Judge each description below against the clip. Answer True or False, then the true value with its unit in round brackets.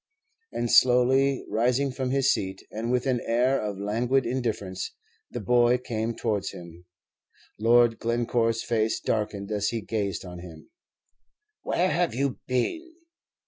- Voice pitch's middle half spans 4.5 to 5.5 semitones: False (3.3 semitones)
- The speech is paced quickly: False (140 wpm)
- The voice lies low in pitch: True (115 Hz)